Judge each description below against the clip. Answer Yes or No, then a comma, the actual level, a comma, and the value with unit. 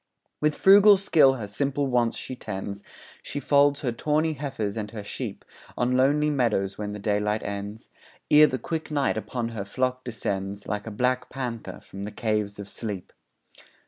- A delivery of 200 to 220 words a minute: No, average, 175 wpm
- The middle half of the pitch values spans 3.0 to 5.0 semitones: No, wide, 5.4 semitones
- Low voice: Yes, low, 120 Hz